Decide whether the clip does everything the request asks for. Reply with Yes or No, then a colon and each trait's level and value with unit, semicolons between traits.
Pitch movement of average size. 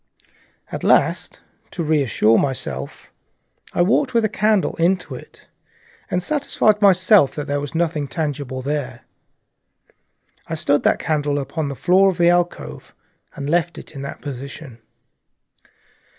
Yes: average, 4.2 semitones